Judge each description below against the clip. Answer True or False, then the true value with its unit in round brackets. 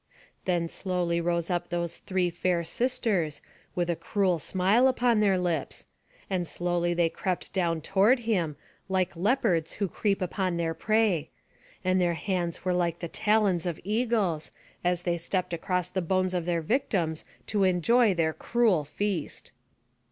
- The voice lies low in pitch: False (180 Hz)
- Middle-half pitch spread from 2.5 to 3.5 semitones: True (2.9 semitones)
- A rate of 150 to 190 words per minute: True (155 wpm)